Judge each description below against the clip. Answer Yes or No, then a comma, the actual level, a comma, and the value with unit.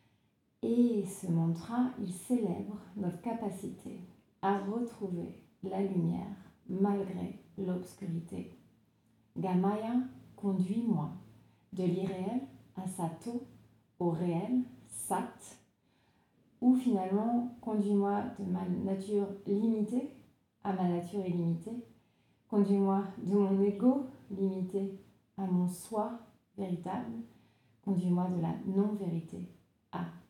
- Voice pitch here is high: Yes, high, 195 Hz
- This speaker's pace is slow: Yes, slow, 95 wpm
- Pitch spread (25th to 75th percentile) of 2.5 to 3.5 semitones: Yes, average, 3.1 semitones